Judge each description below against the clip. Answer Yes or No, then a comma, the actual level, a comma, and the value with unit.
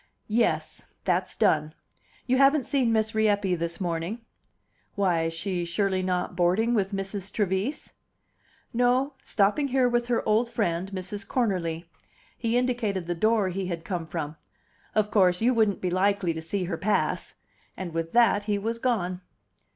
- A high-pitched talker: Yes, high, 195 Hz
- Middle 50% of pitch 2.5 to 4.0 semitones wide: No, average, 4.5 semitones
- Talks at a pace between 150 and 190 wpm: Yes, average, 155 wpm